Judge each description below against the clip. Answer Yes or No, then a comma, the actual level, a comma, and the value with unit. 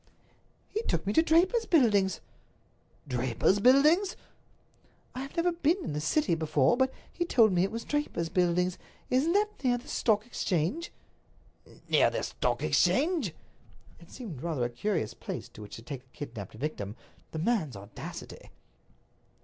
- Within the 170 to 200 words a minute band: No, average, 155 wpm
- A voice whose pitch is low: No, high, 200 Hz